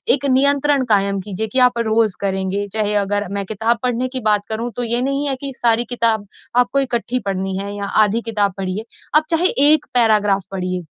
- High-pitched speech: Yes, high, 220 Hz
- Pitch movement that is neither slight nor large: Yes, average, 3.7 semitones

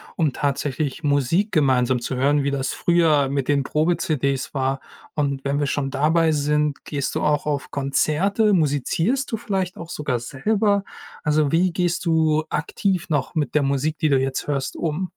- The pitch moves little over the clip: No, average, 3.3 semitones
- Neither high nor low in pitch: Yes, medium, 150 Hz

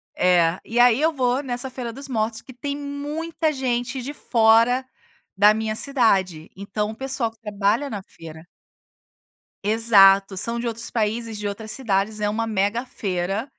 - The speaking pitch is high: Yes, high, 225 Hz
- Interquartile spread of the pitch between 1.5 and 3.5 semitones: No, average, 3.9 semitones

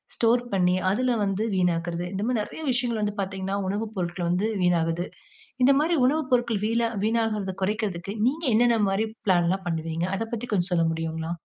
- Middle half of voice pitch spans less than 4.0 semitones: No, average, 4.6 semitones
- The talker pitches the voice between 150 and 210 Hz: Yes, high, 195 Hz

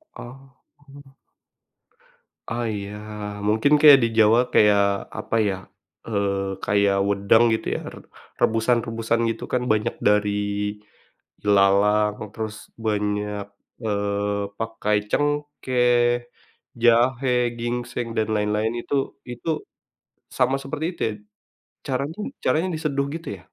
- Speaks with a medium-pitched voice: No, low, 115 Hz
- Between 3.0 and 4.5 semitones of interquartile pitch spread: Yes, average, 3.7 semitones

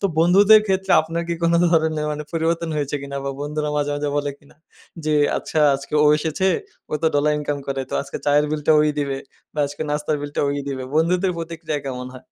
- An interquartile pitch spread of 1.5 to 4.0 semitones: Yes, narrow, 2.4 semitones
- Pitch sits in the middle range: Yes, medium, 150 Hz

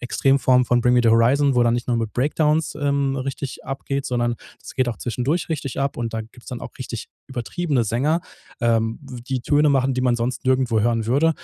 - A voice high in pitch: No, low, 125 Hz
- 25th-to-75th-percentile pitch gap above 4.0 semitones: No, average, 2.7 semitones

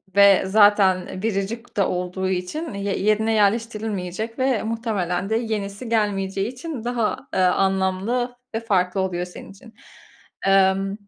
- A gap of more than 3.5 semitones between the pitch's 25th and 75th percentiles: No, average, 3.0 semitones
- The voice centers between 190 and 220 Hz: Yes, high, 200 Hz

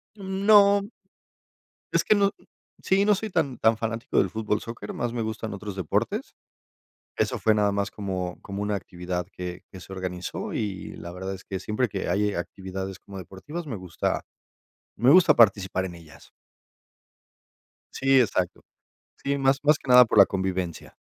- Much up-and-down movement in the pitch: Yes, wide, 6.2 semitones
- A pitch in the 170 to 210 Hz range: No, low, 105 Hz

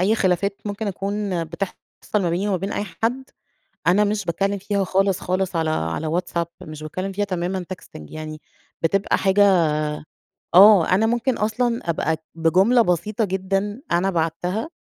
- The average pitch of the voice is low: No, high, 190 Hz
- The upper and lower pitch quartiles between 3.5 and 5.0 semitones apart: No, average, 3.1 semitones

